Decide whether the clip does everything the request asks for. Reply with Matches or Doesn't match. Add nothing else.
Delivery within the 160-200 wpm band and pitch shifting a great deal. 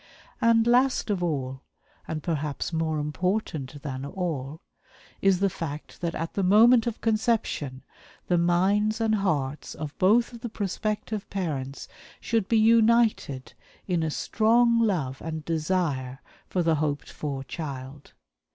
Doesn't match